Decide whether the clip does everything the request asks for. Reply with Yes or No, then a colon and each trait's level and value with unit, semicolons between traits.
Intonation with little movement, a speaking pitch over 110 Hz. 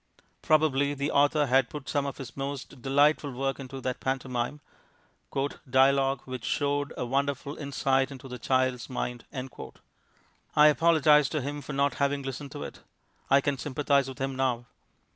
Yes: narrow, 1.5 semitones; low, 135 Hz